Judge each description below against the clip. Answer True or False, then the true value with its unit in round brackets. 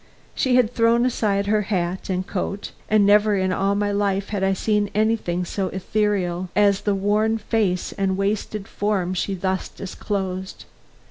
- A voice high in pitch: True (200 Hz)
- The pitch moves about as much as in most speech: False (1.9 semitones)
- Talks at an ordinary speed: True (160 wpm)